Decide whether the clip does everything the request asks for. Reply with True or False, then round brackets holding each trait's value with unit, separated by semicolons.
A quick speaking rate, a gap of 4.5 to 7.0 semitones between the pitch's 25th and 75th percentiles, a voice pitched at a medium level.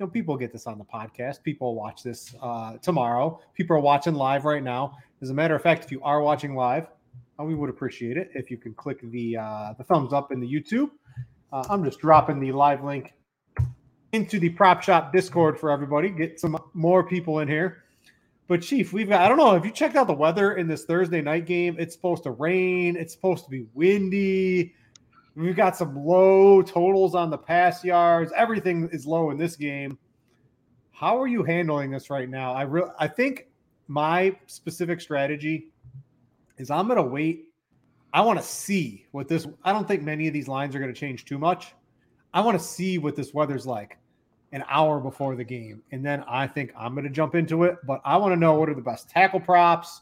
True (210 wpm; 4.8 semitones; 155 Hz)